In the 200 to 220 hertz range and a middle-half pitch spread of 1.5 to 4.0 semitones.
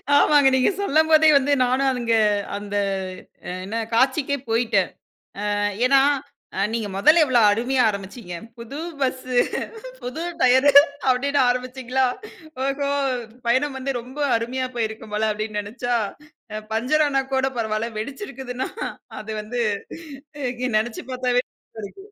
No: very high, 250 Hz; average, 3.2 semitones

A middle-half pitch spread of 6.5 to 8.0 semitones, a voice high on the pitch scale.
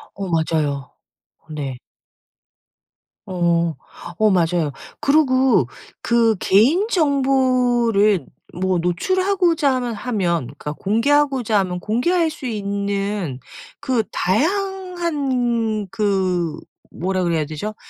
Yes: wide, 7.1 semitones; high, 215 Hz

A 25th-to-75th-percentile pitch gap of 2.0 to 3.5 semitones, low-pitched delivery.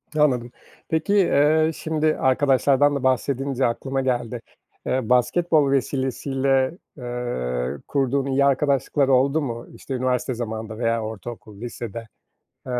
Yes: average, 2.7 semitones; low, 130 Hz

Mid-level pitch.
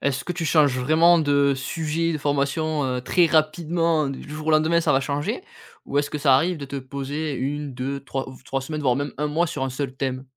Yes: medium, 145 Hz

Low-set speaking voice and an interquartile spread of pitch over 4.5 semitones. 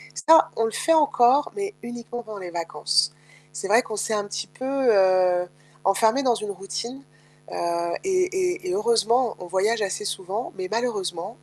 No: high, 220 Hz; average, 5.2 semitones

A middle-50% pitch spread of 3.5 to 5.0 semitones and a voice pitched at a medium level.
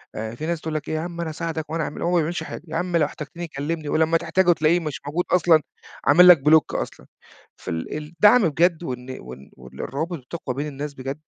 No: average, 2.8 semitones; medium, 155 Hz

